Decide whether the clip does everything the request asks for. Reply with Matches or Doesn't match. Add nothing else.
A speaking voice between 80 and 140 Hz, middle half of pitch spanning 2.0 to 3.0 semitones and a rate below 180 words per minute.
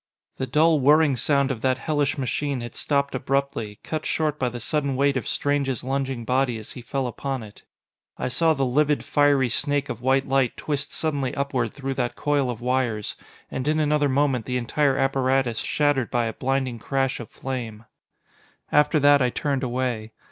Doesn't match